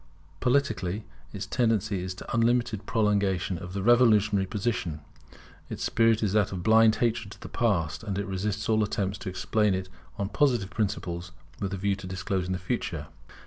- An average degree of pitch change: Yes, average, 3.0 semitones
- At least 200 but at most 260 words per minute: No, average, 175 wpm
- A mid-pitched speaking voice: No, low, 100 Hz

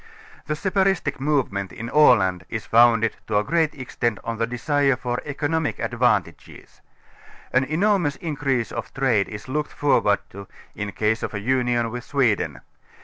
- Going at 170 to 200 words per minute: No, average, 155 wpm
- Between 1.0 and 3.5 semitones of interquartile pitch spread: No, average, 4.9 semitones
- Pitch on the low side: Yes, low, 125 Hz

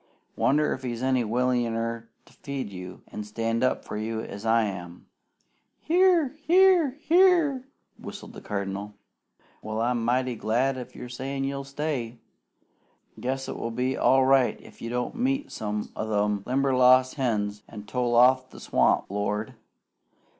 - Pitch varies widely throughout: No, average, 3.8 semitones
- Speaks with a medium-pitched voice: No, low, 125 Hz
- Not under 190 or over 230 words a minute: No, average, 155 wpm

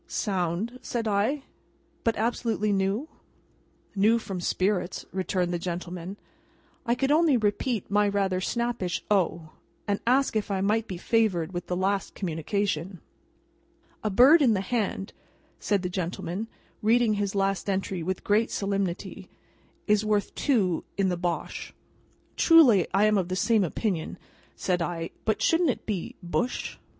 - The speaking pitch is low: No, high, 200 Hz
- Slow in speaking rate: No, average, 150 wpm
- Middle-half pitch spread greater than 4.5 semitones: No, average, 3.6 semitones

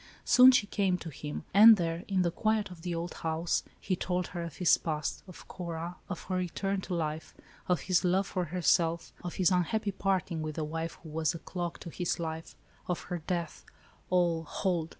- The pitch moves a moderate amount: No, narrow, 2.1 semitones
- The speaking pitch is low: No, medium, 175 Hz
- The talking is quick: Yes, fast, 210 wpm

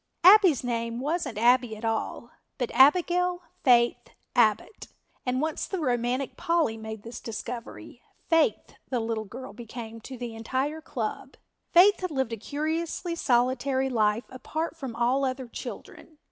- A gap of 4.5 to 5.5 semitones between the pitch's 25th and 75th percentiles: Yes, average, 5.2 semitones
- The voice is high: Yes, very high, 255 Hz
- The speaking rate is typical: Yes, average, 145 wpm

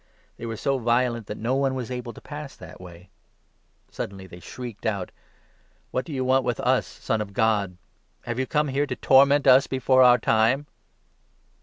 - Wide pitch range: No, average, 3.2 semitones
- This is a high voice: No, low, 125 Hz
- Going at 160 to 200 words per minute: Yes, average, 195 wpm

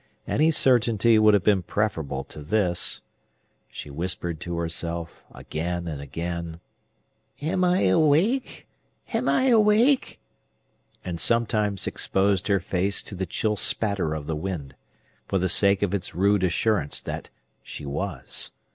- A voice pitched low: Yes, very low, 95 Hz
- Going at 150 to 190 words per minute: No, slow, 135 wpm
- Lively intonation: No, average, 4.5 semitones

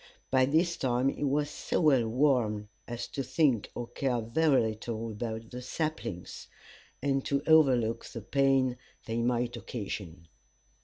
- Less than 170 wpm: Yes, average, 145 wpm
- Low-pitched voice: Yes, low, 125 Hz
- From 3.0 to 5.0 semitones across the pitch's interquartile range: Yes, average, 3.5 semitones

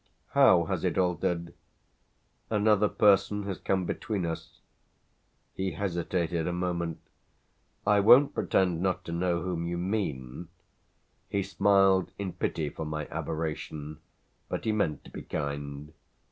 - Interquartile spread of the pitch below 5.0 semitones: Yes, average, 3.1 semitones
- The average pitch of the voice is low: Yes, very low, 90 Hz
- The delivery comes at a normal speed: No, slow, 130 wpm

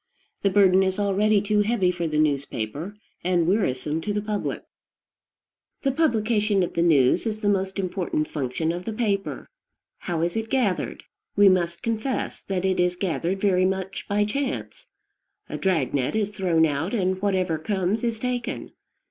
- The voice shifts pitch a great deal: No, average, 3.5 semitones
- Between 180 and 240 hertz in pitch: Yes, high, 190 Hz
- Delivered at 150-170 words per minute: Yes, average, 165 wpm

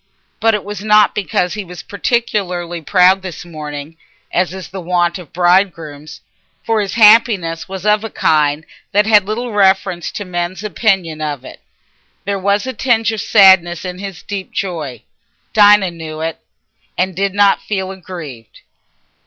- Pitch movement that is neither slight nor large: Yes, average, 3.3 semitones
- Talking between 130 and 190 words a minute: Yes, average, 160 wpm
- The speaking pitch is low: No, high, 190 Hz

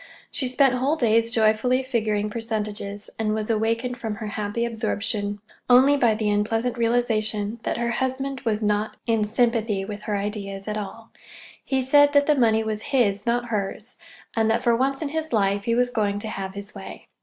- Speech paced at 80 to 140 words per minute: No, average, 190 wpm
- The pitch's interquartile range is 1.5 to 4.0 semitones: Yes, average, 2.9 semitones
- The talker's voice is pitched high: Yes, high, 225 Hz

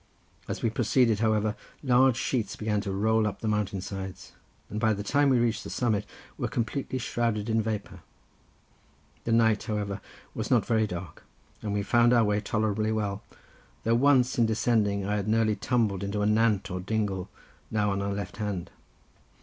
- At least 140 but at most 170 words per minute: No, average, 180 wpm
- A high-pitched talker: No, low, 110 Hz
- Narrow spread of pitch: Yes, narrow, 2.1 semitones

